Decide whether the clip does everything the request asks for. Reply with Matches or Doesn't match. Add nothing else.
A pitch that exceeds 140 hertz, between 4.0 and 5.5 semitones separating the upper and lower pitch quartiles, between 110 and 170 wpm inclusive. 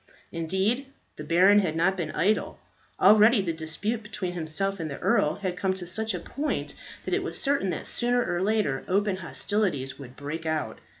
Doesn't match